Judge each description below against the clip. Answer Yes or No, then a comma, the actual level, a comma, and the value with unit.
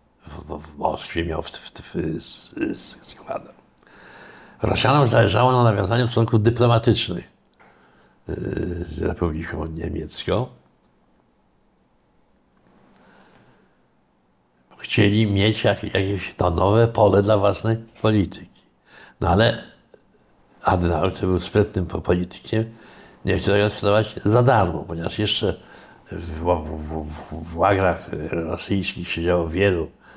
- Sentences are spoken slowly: Yes, slow, 95 wpm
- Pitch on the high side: No, very low, 95 Hz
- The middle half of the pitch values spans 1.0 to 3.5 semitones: No, average, 4.3 semitones